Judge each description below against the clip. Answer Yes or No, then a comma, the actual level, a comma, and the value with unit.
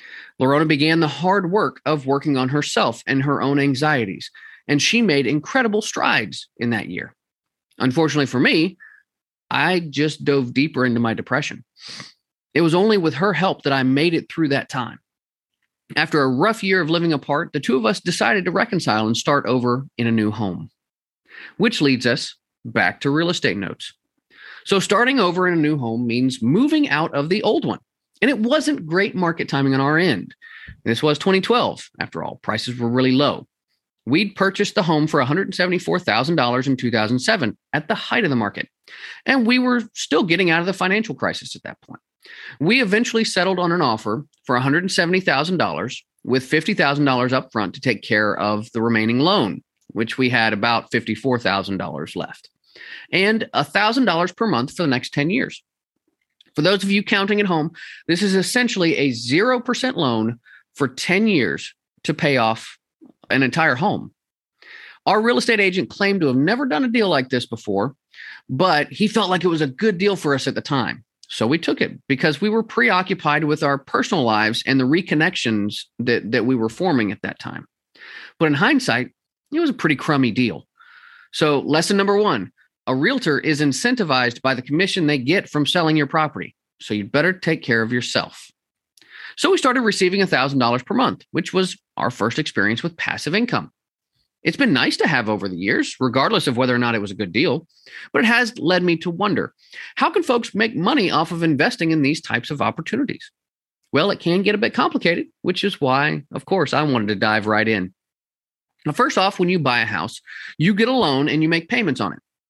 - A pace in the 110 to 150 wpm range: No, average, 195 wpm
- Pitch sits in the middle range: Yes, medium, 155 Hz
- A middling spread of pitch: No, wide, 7.3 semitones